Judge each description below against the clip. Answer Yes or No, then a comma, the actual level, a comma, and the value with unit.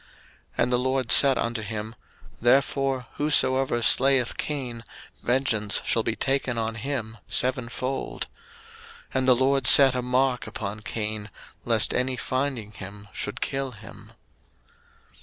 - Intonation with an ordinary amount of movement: Yes, average, 3.1 semitones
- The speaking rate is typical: No, slow, 130 wpm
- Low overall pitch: Yes, low, 125 Hz